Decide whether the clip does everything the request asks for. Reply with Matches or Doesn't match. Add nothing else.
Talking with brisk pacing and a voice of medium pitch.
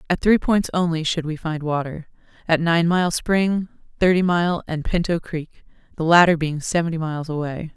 Doesn't match